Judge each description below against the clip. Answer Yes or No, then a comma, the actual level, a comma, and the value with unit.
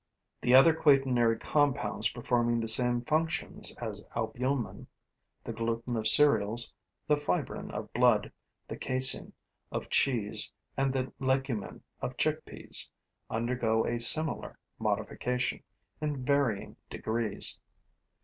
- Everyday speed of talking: No, slow, 110 wpm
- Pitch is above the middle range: No, low, 125 Hz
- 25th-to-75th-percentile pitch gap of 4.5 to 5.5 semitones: No, average, 2.9 semitones